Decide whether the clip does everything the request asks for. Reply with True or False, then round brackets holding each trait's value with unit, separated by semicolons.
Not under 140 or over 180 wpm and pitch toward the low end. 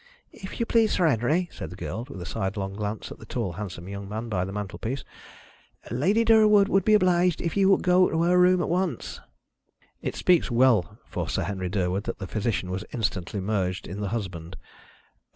False (200 wpm; 115 Hz)